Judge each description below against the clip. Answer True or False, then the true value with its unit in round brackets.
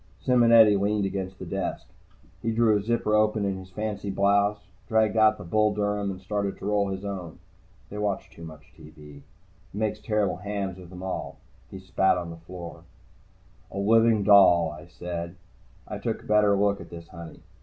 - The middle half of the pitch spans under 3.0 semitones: True (2.6 semitones)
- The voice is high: False (100 Hz)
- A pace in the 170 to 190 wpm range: True (185 wpm)